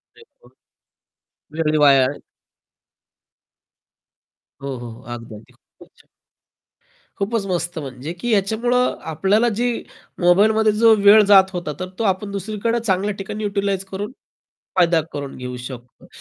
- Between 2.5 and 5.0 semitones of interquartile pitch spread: No, wide, 5.4 semitones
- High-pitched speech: Yes, high, 195 Hz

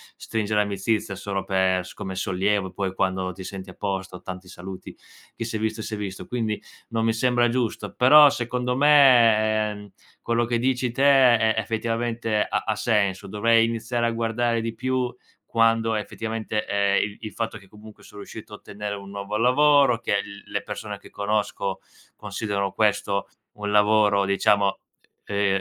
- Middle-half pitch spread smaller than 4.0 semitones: Yes, narrow, 2.6 semitones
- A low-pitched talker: Yes, low, 110 Hz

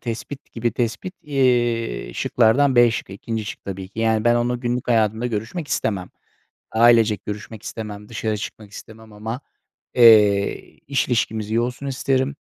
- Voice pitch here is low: Yes, low, 115 Hz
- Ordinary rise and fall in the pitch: No, narrow, 2.3 semitones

